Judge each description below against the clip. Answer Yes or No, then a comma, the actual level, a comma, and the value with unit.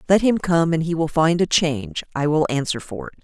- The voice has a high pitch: No, medium, 160 Hz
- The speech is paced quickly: Yes, fast, 260 wpm